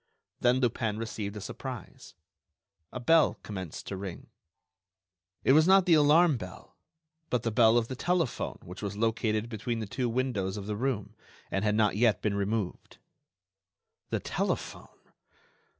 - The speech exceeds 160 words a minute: No, average, 150 wpm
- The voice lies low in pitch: Yes, low, 115 Hz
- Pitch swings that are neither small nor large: Yes, average, 3.8 semitones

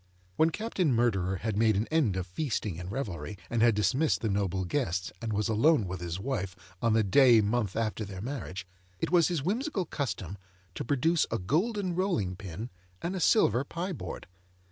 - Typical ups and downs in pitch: No, wide, 8.1 semitones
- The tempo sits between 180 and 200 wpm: Yes, average, 190 wpm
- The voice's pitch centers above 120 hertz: No, low, 115 Hz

